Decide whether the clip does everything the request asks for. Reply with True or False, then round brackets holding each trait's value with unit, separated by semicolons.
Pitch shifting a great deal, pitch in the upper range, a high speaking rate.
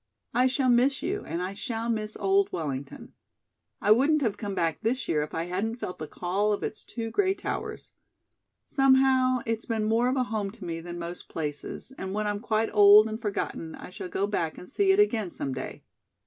True (5.8 semitones; 215 Hz; 210 wpm)